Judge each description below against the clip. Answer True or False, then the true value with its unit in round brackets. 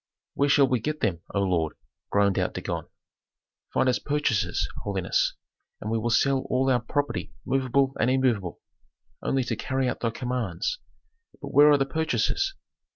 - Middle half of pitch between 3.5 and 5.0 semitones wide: True (4.1 semitones)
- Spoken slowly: False (160 wpm)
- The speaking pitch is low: True (130 Hz)